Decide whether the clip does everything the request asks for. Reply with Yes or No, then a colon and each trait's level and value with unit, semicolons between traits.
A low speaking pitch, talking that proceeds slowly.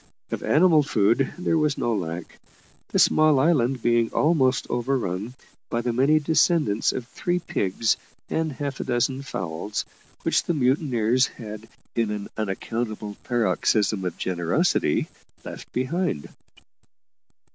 Yes: low, 120 Hz; slow, 125 wpm